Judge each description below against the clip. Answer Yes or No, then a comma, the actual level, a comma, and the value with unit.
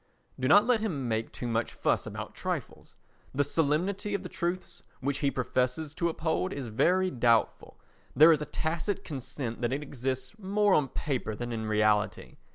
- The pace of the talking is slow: No, average, 175 wpm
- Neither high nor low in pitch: Yes, medium, 145 Hz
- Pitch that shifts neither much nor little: No, wide, 6.4 semitones